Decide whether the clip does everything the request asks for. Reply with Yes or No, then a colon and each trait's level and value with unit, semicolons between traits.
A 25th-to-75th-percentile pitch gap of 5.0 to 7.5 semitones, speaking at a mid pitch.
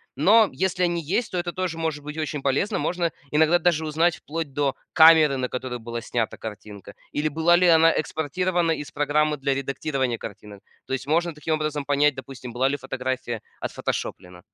No: average, 3.7 semitones; medium, 150 Hz